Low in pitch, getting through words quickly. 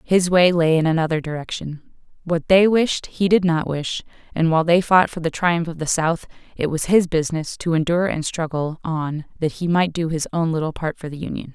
No: medium, 165 Hz; fast, 225 wpm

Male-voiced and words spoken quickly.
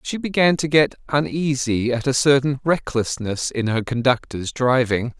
No: male; average, 150 wpm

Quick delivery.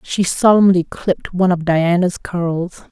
No: average, 145 wpm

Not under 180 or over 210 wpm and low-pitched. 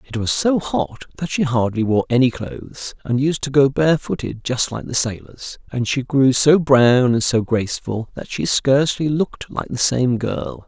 Yes: average, 195 wpm; low, 130 Hz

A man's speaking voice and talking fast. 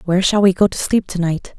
No: female; fast, 305 wpm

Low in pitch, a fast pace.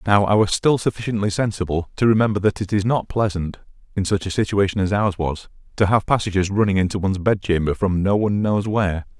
Yes: low, 100 Hz; fast, 215 wpm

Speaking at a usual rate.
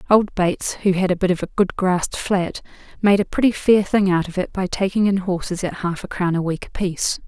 No: fast, 250 wpm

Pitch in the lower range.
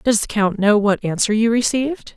No: high, 220 Hz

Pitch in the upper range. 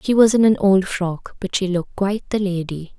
Yes: high, 195 Hz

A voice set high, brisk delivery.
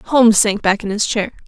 Yes: high, 210 Hz; fast, 245 wpm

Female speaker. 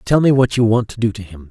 No: male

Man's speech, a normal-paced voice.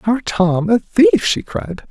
Yes: male; average, 190 wpm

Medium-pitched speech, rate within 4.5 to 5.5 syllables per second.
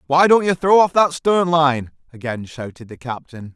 Yes: medium, 150 Hz; 4.7 syllables/s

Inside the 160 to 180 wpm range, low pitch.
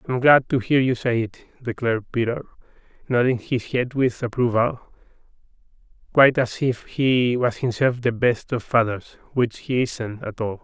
Yes: average, 165 wpm; low, 120 Hz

